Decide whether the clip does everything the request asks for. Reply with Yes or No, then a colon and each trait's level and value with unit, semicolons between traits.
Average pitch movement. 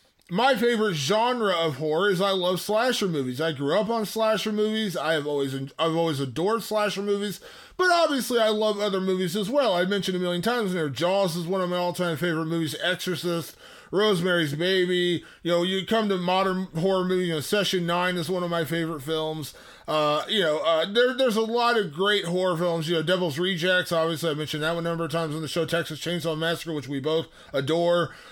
Yes: average, 4.0 semitones